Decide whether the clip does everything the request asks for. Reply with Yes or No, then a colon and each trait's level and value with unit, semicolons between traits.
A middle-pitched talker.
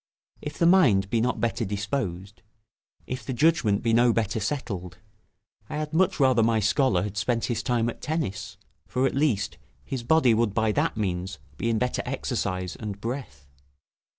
No: low, 115 Hz